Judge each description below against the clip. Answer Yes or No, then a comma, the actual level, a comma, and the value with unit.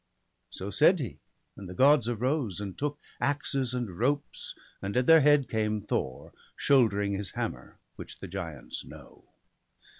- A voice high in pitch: No, low, 120 Hz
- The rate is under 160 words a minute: Yes, average, 150 wpm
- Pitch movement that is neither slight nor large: No, wide, 5.9 semitones